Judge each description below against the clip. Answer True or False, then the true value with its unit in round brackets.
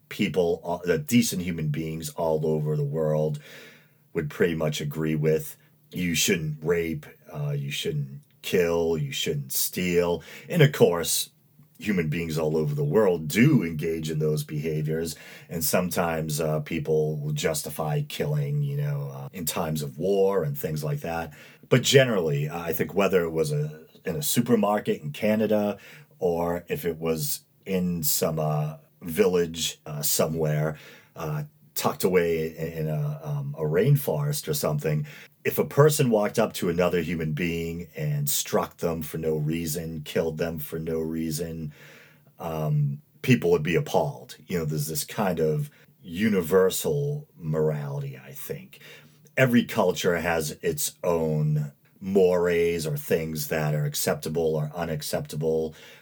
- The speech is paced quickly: False (150 wpm)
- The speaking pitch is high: False (85 Hz)